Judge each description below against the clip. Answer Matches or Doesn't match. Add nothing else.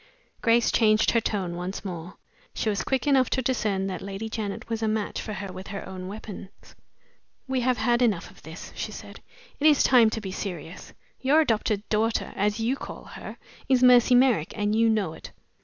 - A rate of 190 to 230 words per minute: Matches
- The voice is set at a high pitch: Matches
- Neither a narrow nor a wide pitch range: Matches